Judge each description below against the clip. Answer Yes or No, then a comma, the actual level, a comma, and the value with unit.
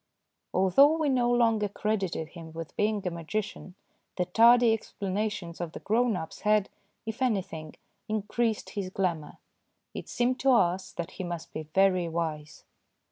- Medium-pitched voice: No, high, 195 Hz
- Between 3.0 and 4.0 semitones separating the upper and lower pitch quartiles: No, average, 4.6 semitones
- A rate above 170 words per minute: No, average, 155 wpm